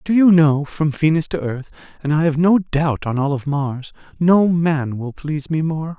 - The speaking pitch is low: No, medium, 155 Hz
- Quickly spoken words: Yes, fast, 220 wpm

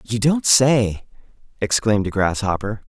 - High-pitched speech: No, low, 110 Hz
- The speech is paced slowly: Yes, slow, 125 wpm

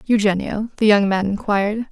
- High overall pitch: Yes, high, 210 Hz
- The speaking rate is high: No, average, 155 wpm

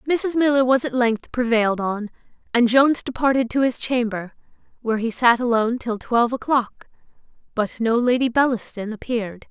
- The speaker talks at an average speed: Yes, average, 160 wpm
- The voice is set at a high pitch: Yes, high, 240 Hz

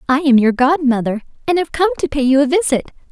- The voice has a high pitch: Yes, very high, 285 Hz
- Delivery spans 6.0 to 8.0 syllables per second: Yes, 6.1 syllables/s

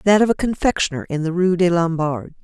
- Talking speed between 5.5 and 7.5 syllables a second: Yes, 5.8 syllables/s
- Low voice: No, medium, 175 Hz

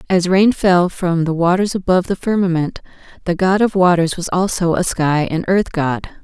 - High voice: No, medium, 180 Hz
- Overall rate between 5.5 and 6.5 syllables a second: No, 4.9 syllables/s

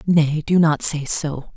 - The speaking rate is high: No, average, 190 wpm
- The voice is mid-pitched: Yes, medium, 155 Hz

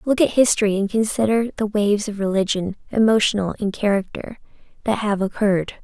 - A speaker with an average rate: Yes, average, 155 wpm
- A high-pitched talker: Yes, high, 210 Hz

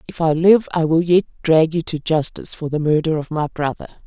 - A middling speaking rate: No, fast, 235 wpm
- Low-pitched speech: No, medium, 160 Hz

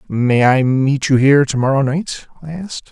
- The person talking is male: Yes, male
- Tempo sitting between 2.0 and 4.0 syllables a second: No, 5.1 syllables/s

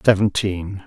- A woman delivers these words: No, male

